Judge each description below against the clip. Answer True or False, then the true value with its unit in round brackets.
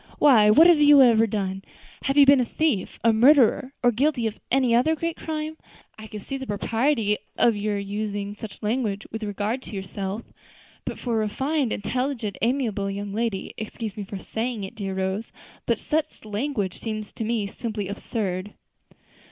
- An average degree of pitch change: True (4.3 semitones)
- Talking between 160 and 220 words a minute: True (175 wpm)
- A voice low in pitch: False (220 Hz)